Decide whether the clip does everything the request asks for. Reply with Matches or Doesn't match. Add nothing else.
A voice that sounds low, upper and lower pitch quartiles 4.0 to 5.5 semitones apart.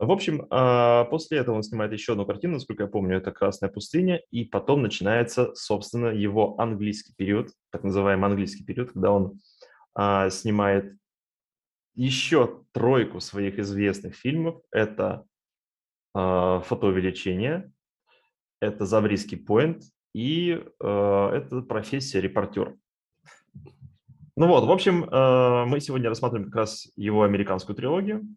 Matches